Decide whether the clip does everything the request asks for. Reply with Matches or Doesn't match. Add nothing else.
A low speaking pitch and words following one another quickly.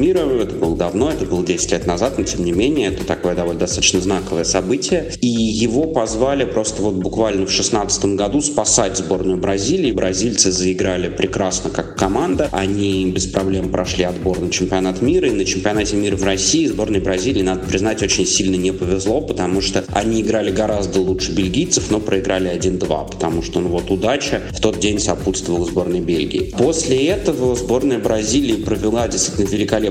Matches